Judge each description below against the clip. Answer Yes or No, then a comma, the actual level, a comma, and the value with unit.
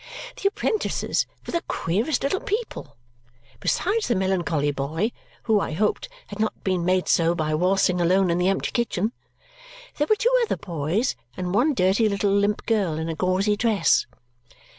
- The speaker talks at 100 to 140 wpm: No, average, 165 wpm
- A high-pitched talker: Yes, high, 195 Hz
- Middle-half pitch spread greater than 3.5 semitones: Yes, average, 4.6 semitones